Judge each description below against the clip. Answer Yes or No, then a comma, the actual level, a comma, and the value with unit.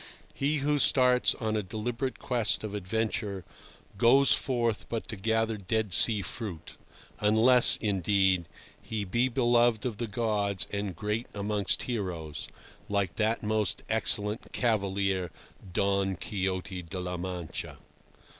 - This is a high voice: No, low, 105 Hz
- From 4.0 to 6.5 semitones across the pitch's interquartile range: No, average, 3.3 semitones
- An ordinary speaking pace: No, slow, 125 wpm